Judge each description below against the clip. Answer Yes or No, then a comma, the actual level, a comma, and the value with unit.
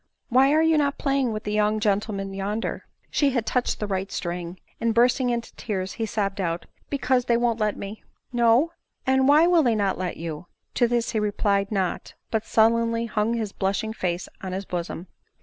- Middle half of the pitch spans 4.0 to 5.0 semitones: No, average, 3.6 semitones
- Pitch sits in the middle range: No, high, 220 Hz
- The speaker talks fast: Yes, fast, 215 wpm